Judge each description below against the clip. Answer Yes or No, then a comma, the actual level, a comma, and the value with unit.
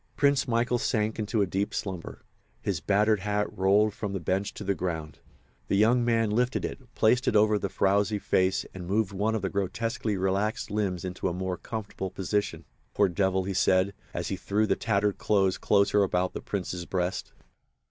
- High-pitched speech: No, low, 100 Hz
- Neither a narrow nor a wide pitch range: No, narrow, 2.3 semitones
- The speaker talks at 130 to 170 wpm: No, average, 185 wpm